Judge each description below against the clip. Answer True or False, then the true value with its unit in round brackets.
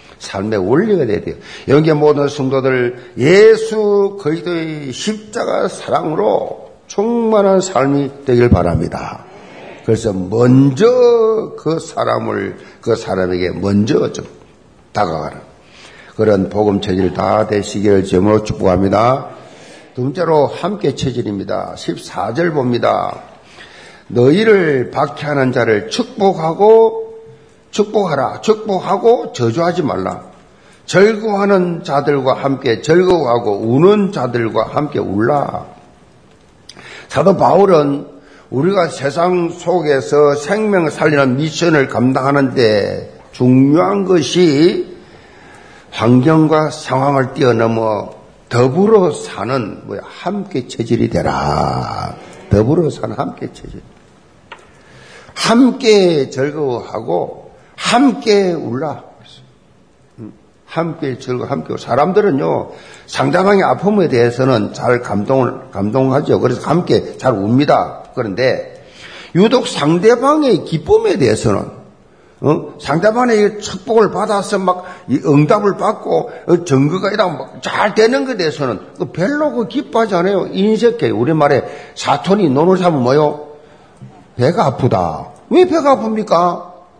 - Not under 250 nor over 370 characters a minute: False (240 characters per minute)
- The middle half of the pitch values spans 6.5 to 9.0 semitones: True (7.7 semitones)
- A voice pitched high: False (160 Hz)